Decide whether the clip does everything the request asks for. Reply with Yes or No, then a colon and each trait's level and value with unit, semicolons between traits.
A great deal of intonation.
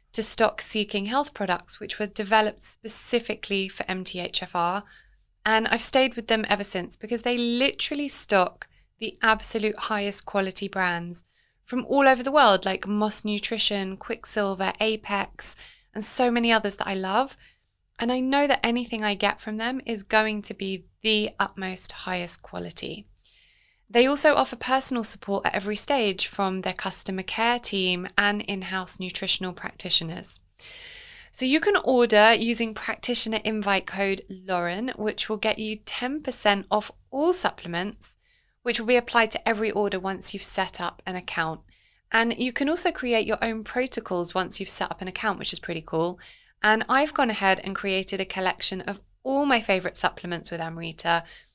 No: average, 3.7 semitones